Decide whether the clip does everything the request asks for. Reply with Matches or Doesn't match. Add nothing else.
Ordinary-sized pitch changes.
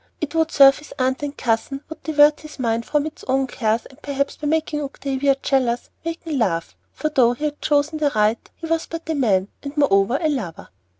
Matches